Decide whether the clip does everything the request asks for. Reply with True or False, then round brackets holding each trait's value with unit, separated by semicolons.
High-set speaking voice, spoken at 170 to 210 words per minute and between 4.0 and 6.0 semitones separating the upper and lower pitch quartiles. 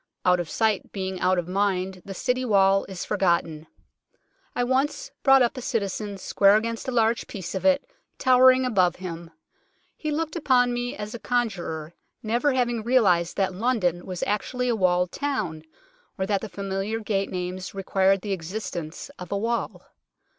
True (200 Hz; 175 wpm; 4.8 semitones)